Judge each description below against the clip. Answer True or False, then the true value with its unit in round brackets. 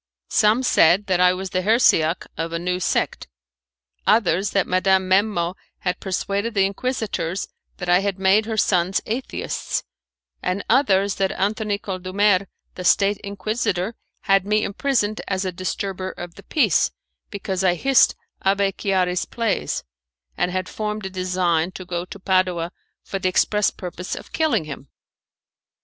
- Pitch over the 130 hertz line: True (190 Hz)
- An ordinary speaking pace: True (150 wpm)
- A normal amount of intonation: False (2.2 semitones)